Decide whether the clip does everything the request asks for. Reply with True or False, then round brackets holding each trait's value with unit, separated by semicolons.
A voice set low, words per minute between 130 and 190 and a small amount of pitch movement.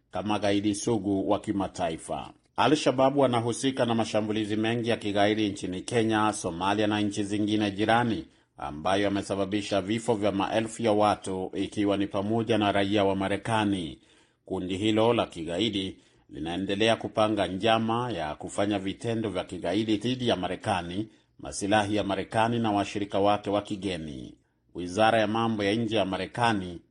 True (105 Hz; 135 wpm; 2.2 semitones)